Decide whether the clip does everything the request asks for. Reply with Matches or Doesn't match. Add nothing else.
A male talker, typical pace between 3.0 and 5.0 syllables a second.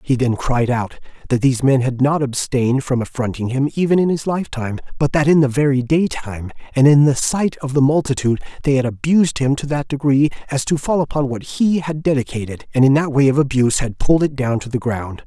Doesn't match